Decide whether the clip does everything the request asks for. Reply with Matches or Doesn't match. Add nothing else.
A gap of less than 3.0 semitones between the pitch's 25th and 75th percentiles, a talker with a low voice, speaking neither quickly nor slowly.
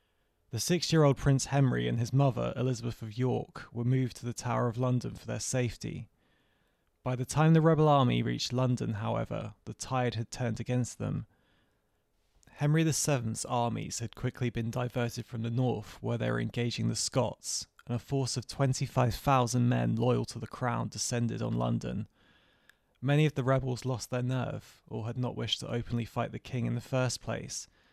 Matches